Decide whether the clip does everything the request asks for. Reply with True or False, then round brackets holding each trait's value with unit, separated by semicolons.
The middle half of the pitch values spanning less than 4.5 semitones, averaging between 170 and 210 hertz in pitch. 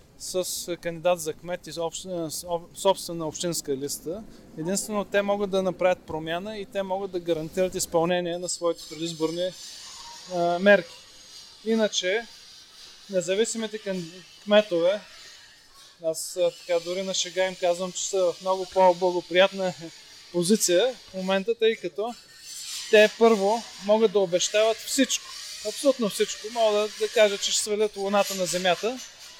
True (3.5 semitones; 185 Hz)